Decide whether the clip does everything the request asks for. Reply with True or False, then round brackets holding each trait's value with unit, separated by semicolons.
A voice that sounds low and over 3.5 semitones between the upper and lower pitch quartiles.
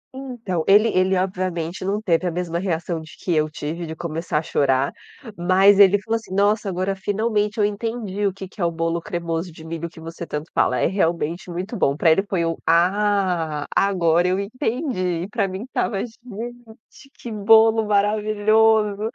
False (190 Hz; 4.0 semitones)